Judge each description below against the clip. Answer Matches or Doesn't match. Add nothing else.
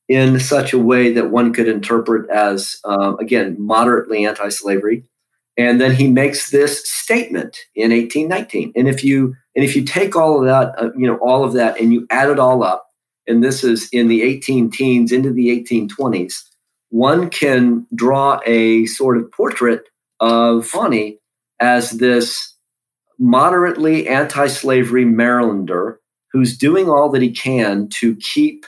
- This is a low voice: Matches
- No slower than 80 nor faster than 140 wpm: Doesn't match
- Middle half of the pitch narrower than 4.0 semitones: Matches